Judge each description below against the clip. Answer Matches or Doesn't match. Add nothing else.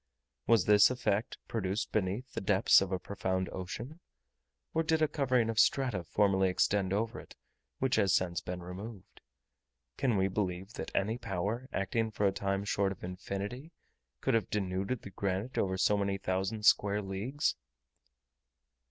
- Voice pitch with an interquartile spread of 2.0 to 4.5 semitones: Matches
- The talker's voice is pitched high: Doesn't match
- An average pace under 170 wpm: Matches